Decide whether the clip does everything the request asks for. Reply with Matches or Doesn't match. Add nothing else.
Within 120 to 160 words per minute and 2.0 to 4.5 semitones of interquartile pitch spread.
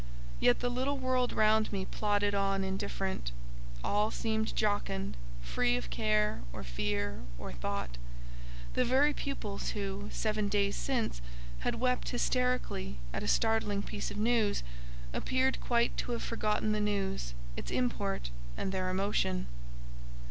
Matches